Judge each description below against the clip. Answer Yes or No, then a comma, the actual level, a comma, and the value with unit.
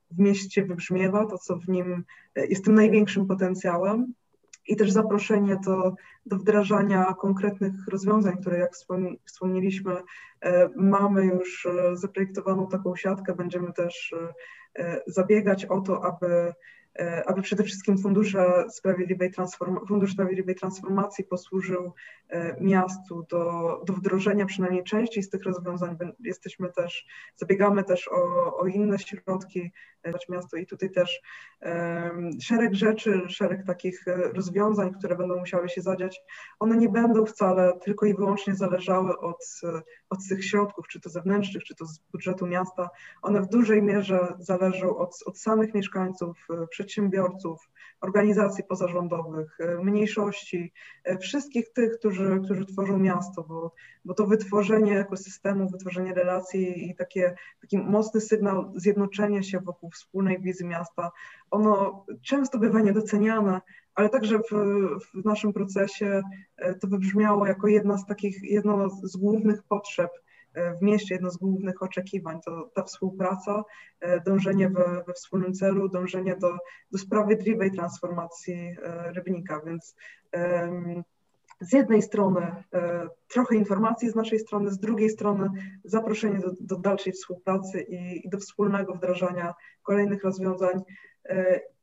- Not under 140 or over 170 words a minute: No, average, 130 wpm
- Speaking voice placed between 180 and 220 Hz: Yes, high, 190 Hz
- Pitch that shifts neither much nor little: No, narrow, 2.3 semitones